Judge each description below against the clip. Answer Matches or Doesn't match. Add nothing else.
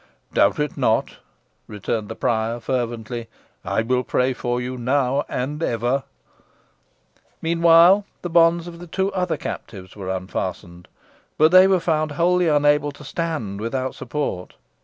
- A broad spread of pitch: Matches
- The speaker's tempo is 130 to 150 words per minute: Matches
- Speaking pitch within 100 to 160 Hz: Matches